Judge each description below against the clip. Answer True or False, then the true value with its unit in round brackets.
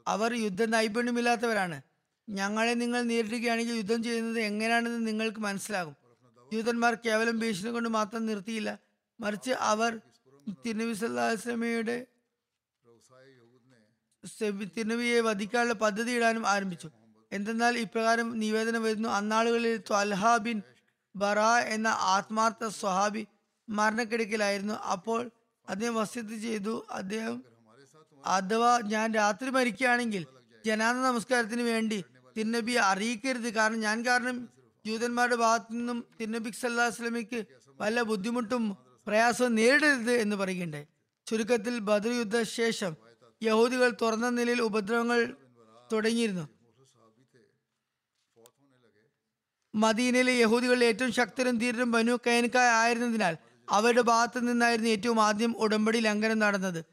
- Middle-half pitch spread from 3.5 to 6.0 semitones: False (2.9 semitones)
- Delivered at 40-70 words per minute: False (90 wpm)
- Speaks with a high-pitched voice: True (225 Hz)